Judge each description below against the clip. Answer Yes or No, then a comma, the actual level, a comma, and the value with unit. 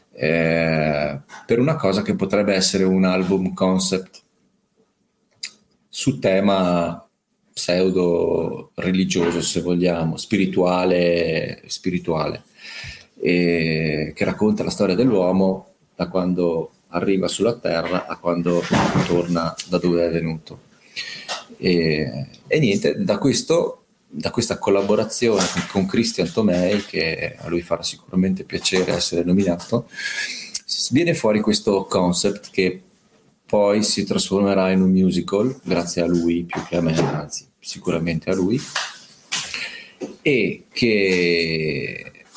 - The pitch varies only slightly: Yes, narrow, 1.8 semitones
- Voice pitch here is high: No, very low, 90 Hz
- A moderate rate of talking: No, slow, 110 wpm